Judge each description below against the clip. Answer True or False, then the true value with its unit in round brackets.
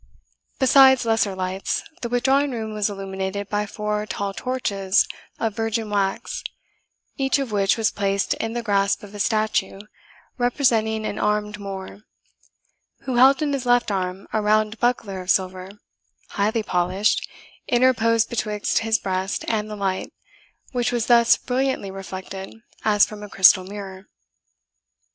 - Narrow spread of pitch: False (3.3 semitones)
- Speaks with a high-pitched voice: True (210 Hz)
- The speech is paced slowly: False (145 wpm)